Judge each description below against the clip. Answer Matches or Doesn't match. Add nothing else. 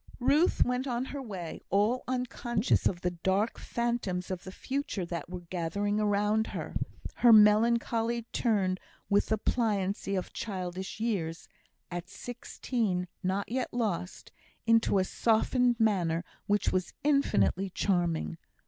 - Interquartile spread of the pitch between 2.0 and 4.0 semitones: Doesn't match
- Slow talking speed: Matches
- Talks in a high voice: Matches